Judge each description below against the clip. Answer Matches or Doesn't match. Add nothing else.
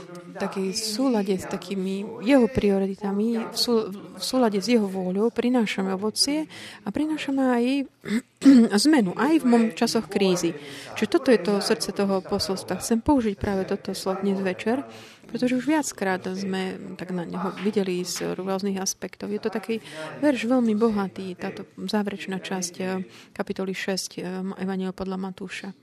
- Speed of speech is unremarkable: Matches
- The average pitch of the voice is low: Doesn't match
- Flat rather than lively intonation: Doesn't match